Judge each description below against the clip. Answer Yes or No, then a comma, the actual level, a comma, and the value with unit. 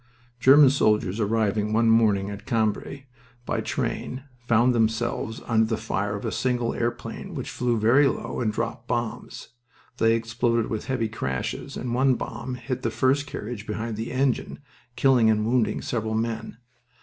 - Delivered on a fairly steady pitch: Yes, narrow, 2.1 semitones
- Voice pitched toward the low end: Yes, low, 115 Hz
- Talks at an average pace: Yes, average, 160 wpm